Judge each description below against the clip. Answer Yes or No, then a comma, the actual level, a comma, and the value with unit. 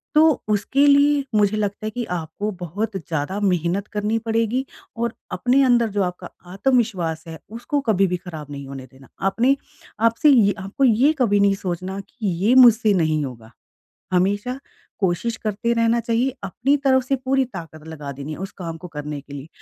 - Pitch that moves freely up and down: Yes, wide, 5.7 semitones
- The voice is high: Yes, high, 205 Hz